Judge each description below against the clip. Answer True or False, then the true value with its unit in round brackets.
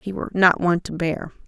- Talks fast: True (245 wpm)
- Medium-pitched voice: True (175 Hz)